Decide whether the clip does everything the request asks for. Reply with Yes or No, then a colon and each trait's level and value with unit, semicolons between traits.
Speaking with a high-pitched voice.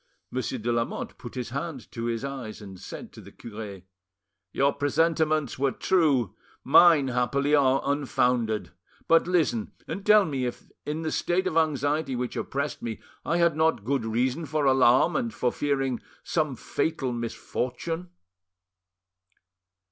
No: low, 135 Hz